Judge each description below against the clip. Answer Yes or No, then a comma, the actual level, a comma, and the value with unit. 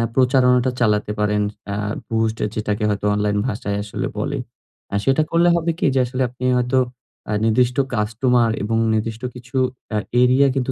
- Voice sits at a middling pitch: No, low, 120 Hz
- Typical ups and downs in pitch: Yes, average, 3.4 semitones